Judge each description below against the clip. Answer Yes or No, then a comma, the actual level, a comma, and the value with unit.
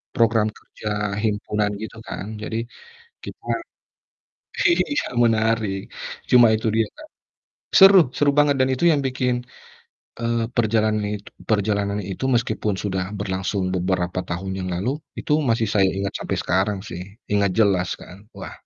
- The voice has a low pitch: Yes, low, 105 Hz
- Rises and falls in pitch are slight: No, average, 3.1 semitones